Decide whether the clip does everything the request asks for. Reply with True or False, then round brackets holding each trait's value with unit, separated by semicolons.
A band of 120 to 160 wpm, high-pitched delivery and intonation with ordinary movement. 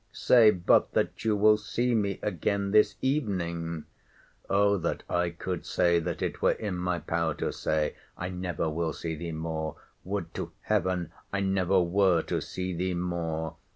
False (155 wpm; 90 Hz; 3.1 semitones)